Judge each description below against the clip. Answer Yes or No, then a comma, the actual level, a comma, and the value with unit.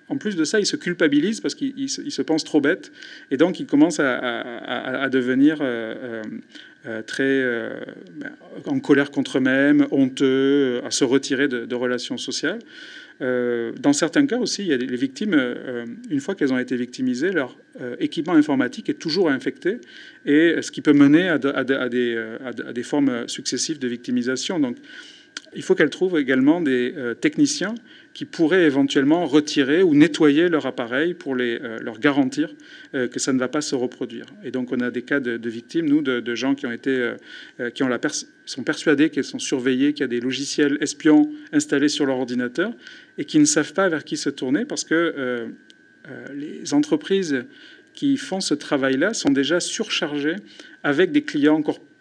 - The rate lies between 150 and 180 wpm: No, average, 195 wpm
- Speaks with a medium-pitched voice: Yes, medium, 145 Hz